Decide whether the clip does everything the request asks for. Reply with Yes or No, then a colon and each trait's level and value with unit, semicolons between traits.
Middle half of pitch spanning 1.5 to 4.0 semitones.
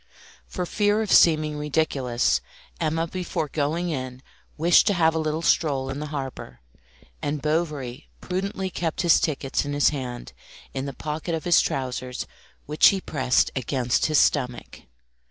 Yes: average, 3.7 semitones